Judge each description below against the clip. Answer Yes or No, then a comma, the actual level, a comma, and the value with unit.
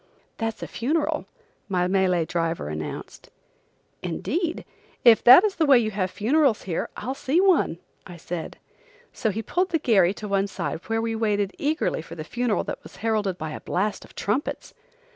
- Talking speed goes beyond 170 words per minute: Yes, average, 180 wpm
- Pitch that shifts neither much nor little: No, wide, 6.1 semitones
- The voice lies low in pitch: No, high, 215 Hz